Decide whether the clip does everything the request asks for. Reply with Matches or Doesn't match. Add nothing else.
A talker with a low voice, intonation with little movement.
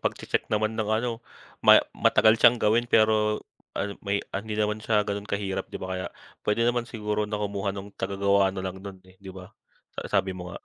Matches